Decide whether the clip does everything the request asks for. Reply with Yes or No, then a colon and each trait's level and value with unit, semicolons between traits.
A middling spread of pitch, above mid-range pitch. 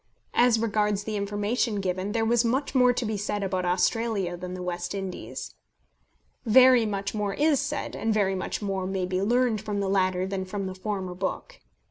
Yes: average, 3.2 semitones; high, 205 Hz